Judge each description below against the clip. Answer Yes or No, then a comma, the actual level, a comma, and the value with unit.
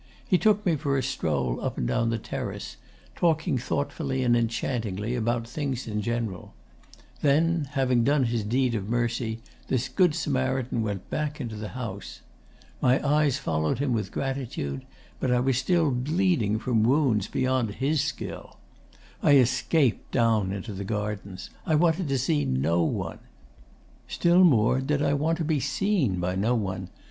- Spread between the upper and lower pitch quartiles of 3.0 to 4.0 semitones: No, average, 4.9 semitones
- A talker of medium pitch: No, low, 125 Hz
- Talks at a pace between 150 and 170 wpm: Yes, average, 160 wpm